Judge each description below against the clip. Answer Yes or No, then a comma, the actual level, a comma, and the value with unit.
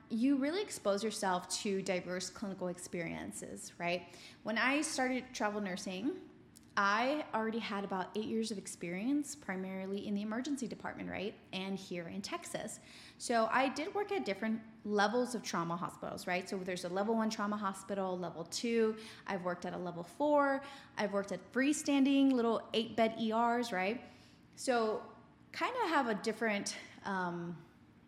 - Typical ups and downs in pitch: Yes, average, 4.5 semitones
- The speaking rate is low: No, average, 160 wpm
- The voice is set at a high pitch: Yes, high, 210 Hz